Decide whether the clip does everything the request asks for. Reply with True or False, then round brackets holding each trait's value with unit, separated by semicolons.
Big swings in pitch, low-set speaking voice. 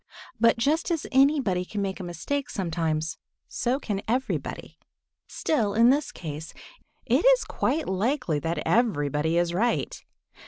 False (7.9 semitones; 205 Hz)